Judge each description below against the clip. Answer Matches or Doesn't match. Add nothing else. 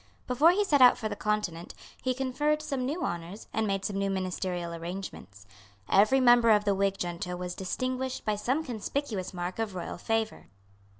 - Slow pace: Doesn't match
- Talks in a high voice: Matches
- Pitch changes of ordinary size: Doesn't match